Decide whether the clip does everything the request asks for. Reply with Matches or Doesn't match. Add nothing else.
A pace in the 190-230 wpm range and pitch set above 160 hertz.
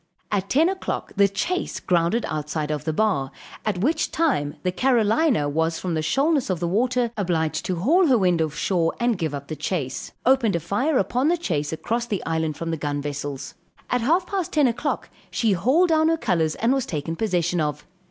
Matches